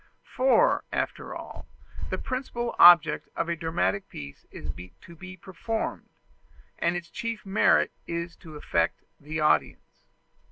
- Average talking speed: No, slow, 130 wpm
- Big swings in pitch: No, average, 5.0 semitones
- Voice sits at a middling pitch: Yes, medium, 170 Hz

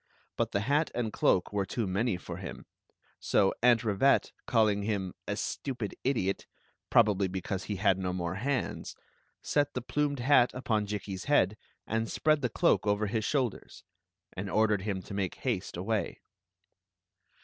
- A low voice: Yes, low, 105 Hz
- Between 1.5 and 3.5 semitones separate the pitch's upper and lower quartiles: No, average, 4.1 semitones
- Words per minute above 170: No, average, 165 wpm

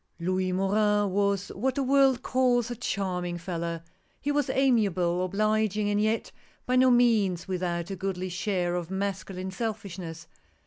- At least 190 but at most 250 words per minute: No, average, 160 wpm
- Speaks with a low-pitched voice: No, high, 195 Hz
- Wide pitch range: No, average, 3.8 semitones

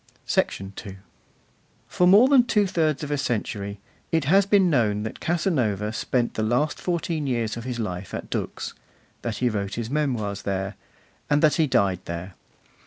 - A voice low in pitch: Yes, low, 120 Hz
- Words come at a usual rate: Yes, average, 170 wpm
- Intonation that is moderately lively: No, wide, 7.5 semitones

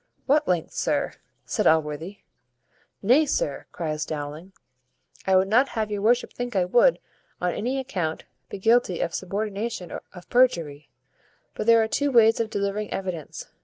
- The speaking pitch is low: No, high, 200 Hz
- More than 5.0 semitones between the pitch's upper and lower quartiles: Yes, wide, 5.4 semitones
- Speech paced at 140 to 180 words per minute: Yes, average, 155 wpm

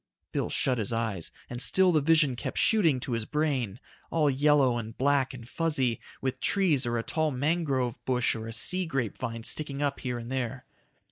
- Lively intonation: No, average, 4.1 semitones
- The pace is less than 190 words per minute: No, average, 195 wpm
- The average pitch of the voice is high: No, low, 130 Hz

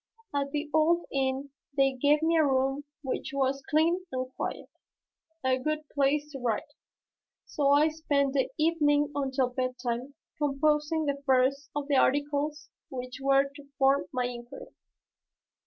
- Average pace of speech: Yes, average, 145 wpm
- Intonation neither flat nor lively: No, narrow, 2.1 semitones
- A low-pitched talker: No, very high, 280 Hz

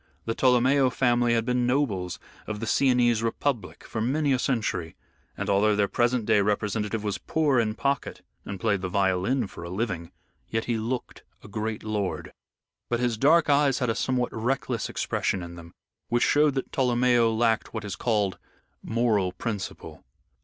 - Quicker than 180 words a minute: No, average, 170 wpm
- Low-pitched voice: Yes, low, 115 Hz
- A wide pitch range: No, average, 3.4 semitones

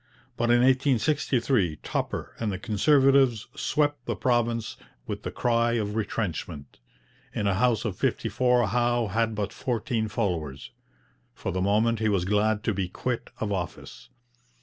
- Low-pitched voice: Yes, low, 115 Hz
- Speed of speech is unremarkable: Yes, average, 150 wpm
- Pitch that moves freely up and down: No, average, 3.2 semitones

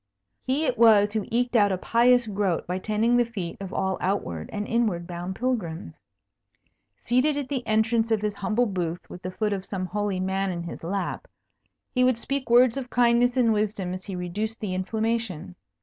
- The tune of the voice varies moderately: Yes, average, 4.2 semitones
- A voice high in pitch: Yes, high, 210 Hz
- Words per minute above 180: Yes, average, 195 wpm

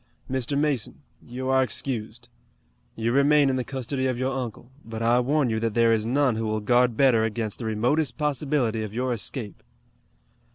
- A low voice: Yes, low, 125 Hz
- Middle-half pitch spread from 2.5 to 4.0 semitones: Yes, average, 3.0 semitones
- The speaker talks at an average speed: Yes, average, 180 wpm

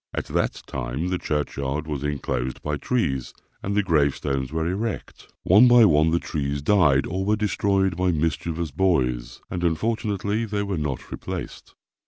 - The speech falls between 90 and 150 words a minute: No, average, 160 wpm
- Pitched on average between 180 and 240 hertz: No, very low, 80 Hz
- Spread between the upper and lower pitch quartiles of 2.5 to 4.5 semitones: No, wide, 5.5 semitones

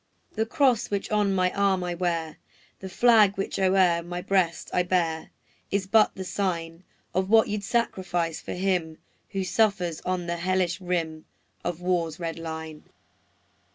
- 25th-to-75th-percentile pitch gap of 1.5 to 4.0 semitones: Yes, narrow, 2.6 semitones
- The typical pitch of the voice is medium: Yes, medium, 180 Hz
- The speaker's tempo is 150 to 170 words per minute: Yes, average, 160 wpm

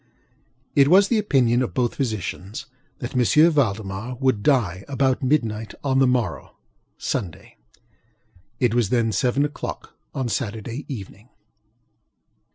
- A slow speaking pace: Yes, slow, 125 wpm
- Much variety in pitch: No, average, 3.8 semitones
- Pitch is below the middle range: Yes, low, 125 Hz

